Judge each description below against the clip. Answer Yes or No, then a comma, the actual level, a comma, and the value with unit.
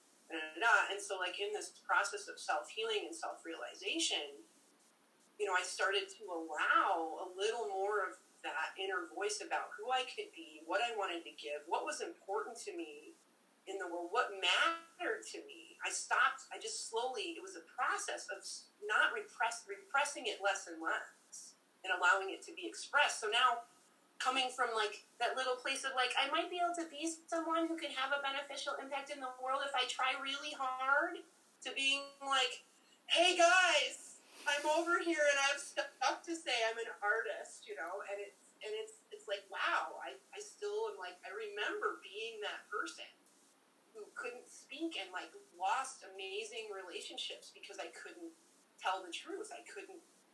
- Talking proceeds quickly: No, average, 180 wpm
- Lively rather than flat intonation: Yes, wide, 7.3 semitones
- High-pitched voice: Yes, very high, 320 Hz